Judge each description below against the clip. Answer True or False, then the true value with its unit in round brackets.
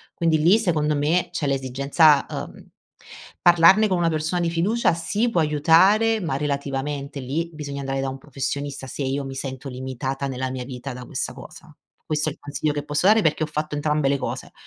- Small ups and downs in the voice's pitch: False (3.4 semitones)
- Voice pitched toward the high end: False (150 Hz)